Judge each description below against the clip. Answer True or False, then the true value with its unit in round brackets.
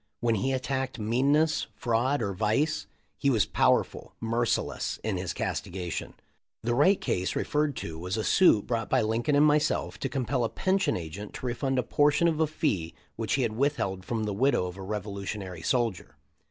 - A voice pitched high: False (115 Hz)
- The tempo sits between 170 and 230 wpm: True (185 wpm)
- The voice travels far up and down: True (5.8 semitones)